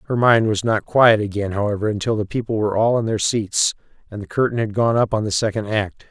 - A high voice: No, low, 110 Hz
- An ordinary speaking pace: No, fast, 245 wpm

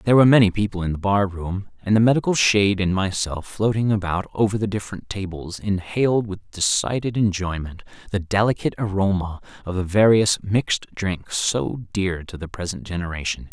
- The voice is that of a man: Yes, male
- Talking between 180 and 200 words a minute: No, average, 170 wpm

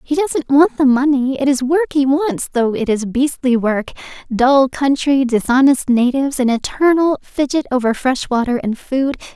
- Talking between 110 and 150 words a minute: No, average, 165 wpm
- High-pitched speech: Yes, very high, 265 Hz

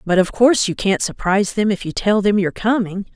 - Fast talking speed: Yes, fast, 250 wpm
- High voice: Yes, high, 200 Hz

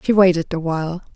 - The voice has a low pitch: No, medium, 175 Hz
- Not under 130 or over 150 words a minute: No, fast, 205 wpm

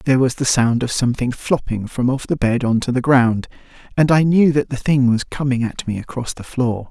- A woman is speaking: No, male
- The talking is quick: Yes, fast, 245 wpm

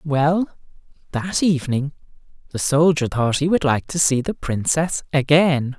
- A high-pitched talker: No, medium, 150 Hz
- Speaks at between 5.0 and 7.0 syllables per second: No, 4.3 syllables/s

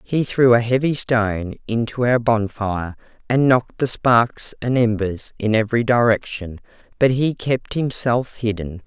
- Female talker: Yes, female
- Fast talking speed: No, average, 150 wpm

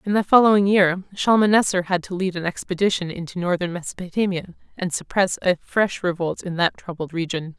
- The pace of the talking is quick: No, average, 175 wpm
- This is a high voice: No, medium, 180 Hz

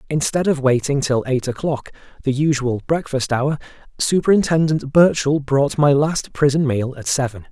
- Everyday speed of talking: Yes, average, 150 wpm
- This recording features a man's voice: Yes, male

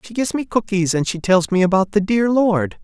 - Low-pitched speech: No, high, 195 Hz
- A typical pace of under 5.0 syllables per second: No, 5.5 syllables/s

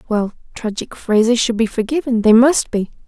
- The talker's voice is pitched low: No, high, 230 Hz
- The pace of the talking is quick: No, average, 175 wpm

